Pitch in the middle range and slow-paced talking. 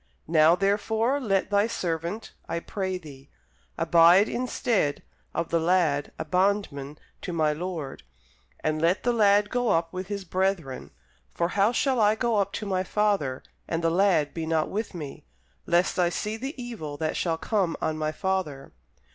No: medium, 180 Hz; average, 170 wpm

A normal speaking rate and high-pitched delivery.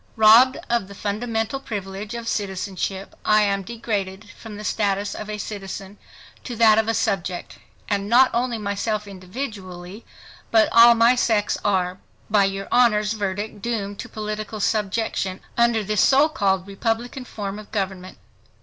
Yes: average, 150 wpm; high, 210 Hz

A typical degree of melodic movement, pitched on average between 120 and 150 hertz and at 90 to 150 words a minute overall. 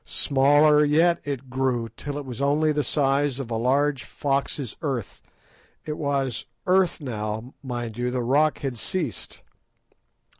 Yes: average, 3.0 semitones; medium, 140 Hz; average, 140 wpm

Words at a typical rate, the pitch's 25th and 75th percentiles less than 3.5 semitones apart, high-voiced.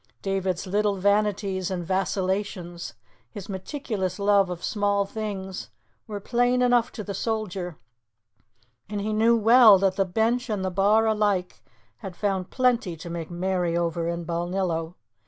Yes: average, 145 wpm; average, 2.8 semitones; high, 195 Hz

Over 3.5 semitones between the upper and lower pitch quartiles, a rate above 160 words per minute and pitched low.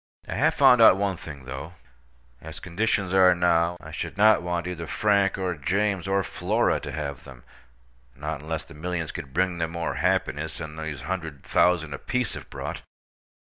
Yes: average, 4.1 semitones; average, 175 wpm; very low, 85 Hz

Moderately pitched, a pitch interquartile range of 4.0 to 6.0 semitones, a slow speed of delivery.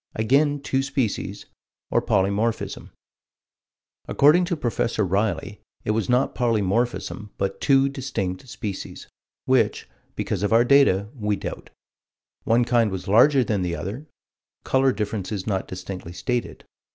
No: low, 110 Hz; average, 5.2 semitones; slow, 125 wpm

